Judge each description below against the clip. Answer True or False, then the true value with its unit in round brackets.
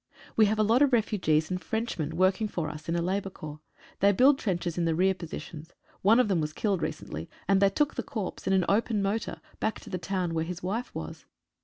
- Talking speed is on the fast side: True (235 wpm)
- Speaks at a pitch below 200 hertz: True (190 Hz)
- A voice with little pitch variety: False (4.3 semitones)